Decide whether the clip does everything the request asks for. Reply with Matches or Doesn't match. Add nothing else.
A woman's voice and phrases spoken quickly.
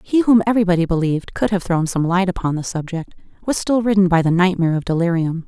Matches